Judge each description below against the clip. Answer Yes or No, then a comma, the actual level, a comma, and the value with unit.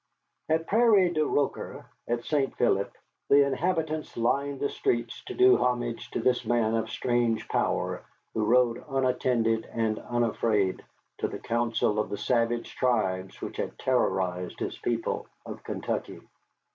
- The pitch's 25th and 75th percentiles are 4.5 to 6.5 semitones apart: No, average, 3.7 semitones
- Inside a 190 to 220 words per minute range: No, average, 145 wpm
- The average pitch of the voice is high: No, low, 120 Hz